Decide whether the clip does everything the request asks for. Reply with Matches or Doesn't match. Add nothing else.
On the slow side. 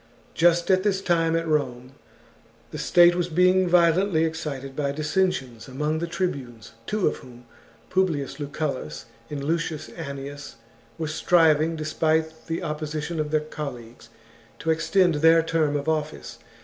Doesn't match